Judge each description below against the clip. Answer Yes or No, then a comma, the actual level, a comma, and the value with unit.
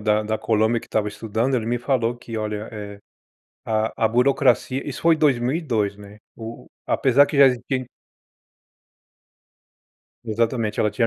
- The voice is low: Yes, low, 115 Hz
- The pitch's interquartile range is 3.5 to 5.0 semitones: No, average, 3.1 semitones